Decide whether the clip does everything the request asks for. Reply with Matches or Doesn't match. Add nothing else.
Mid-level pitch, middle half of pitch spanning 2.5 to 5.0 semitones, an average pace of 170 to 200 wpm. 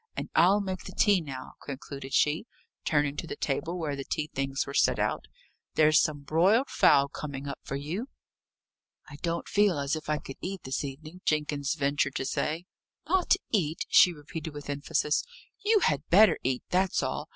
Matches